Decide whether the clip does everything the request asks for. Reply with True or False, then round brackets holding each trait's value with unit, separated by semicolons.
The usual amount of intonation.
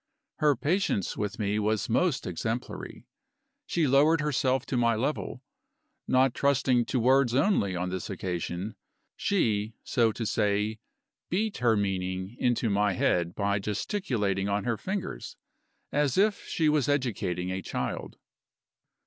False (5.7 semitones)